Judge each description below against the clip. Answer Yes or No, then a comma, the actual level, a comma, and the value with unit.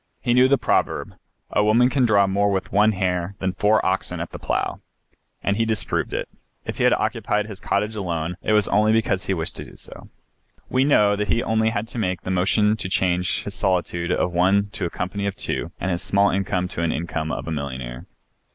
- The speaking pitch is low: Yes, low, 100 Hz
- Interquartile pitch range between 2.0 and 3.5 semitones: Yes, average, 3.0 semitones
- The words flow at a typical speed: No, fast, 220 wpm